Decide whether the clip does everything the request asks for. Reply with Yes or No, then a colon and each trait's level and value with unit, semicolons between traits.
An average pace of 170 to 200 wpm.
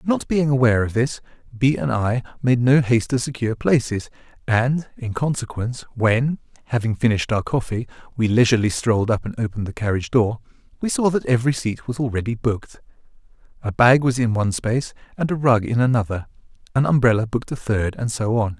Yes: average, 185 wpm